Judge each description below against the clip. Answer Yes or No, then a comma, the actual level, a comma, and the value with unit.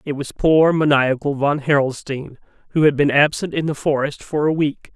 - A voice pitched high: No, medium, 145 Hz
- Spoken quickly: No, average, 195 wpm